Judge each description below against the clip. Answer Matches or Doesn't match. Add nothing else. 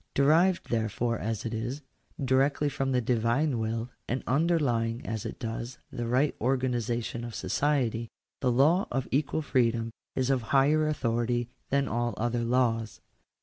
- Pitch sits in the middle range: Doesn't match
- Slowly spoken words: Doesn't match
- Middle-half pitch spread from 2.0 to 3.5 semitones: Matches